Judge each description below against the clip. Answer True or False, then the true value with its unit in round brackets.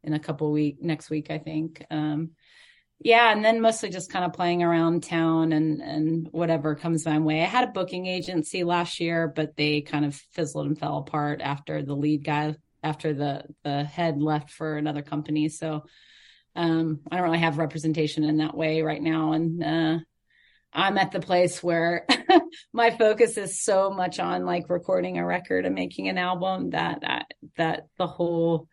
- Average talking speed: True (190 wpm)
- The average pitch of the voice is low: False (160 Hz)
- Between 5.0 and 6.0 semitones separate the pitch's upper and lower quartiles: False (2.8 semitones)